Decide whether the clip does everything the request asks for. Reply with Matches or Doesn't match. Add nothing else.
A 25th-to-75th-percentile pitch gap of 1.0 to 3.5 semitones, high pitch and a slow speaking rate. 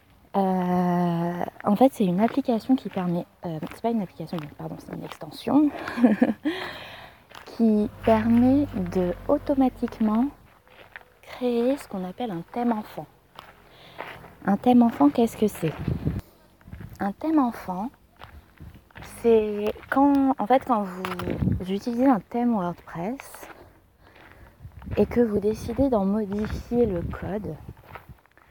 Doesn't match